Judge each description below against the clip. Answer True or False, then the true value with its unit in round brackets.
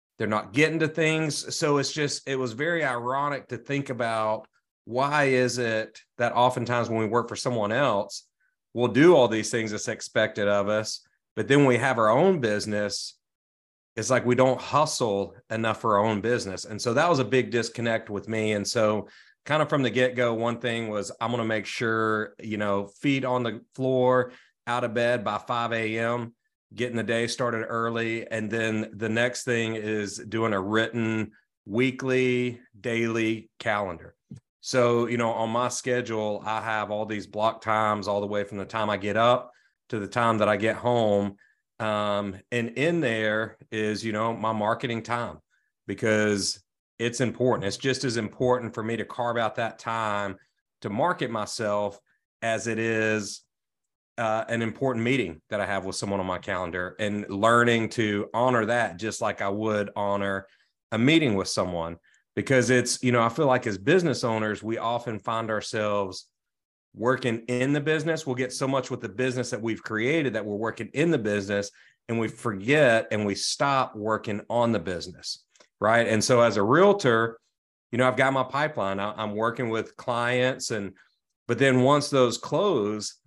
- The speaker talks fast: False (185 wpm)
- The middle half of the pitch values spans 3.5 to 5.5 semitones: False (2.8 semitones)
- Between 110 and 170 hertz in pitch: True (115 Hz)